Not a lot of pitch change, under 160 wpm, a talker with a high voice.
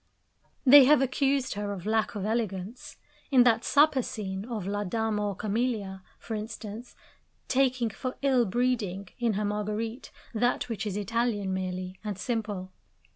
No: average, 3.5 semitones; average, 150 wpm; high, 220 Hz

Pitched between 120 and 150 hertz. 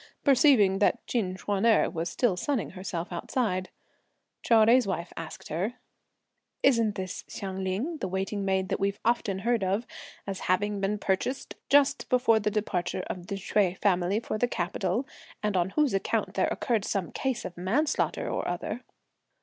No: high, 200 Hz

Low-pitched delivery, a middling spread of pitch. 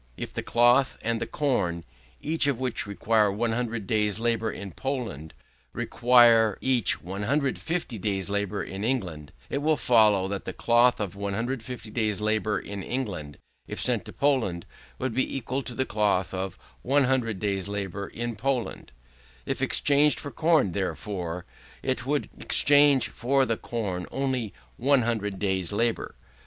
Yes: low, 115 Hz; average, 4.5 semitones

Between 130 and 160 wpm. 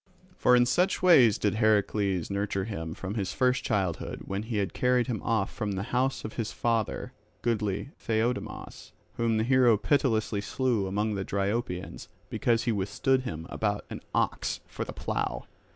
No: average, 170 wpm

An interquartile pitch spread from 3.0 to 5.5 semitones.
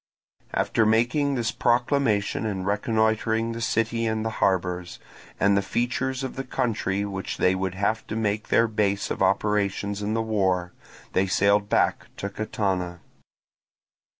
No: narrow, 2.5 semitones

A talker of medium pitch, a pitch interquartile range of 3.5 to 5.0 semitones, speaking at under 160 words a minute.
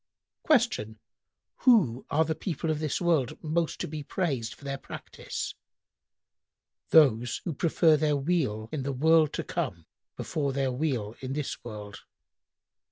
Yes: medium, 145 Hz; average, 4.2 semitones; average, 140 wpm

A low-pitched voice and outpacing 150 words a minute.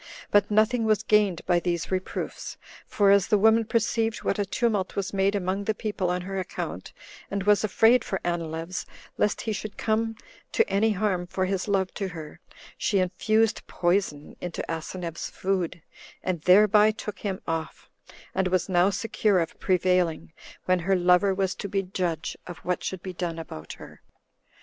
No: high, 190 Hz; average, 175 wpm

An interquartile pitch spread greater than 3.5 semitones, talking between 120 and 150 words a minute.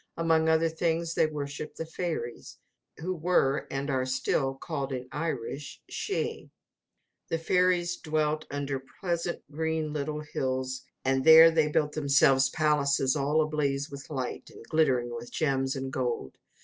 No: average, 3.1 semitones; average, 145 wpm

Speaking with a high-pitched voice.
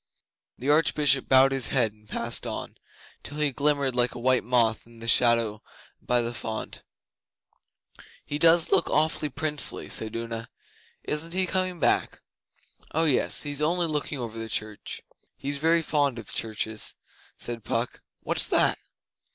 No: low, 130 Hz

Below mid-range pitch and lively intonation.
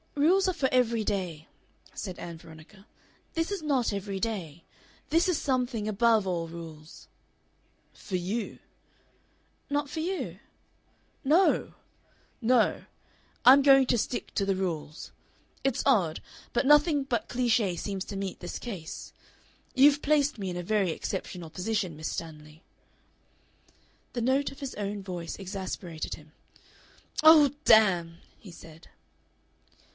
No: high, 210 Hz; wide, 7.4 semitones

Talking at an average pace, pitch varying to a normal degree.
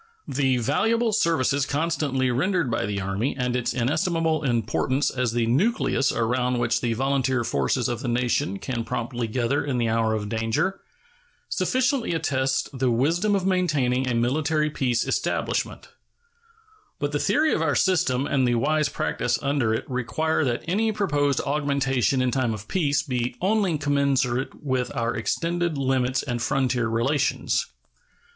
Yes: average, 150 wpm; average, 4.1 semitones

